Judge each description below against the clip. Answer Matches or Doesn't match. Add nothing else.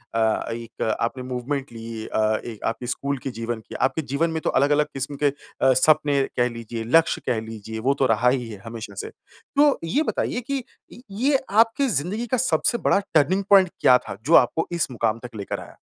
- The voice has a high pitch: Doesn't match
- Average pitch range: Doesn't match